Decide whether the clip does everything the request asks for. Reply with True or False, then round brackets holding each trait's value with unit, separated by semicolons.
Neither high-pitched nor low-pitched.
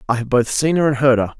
False (130 Hz)